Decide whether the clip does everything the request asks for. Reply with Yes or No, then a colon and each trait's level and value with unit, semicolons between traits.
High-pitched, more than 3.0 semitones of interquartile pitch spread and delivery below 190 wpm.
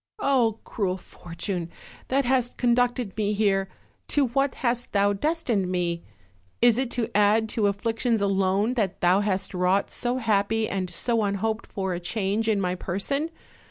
Yes: high, 210 Hz; average, 3.7 semitones; average, 160 wpm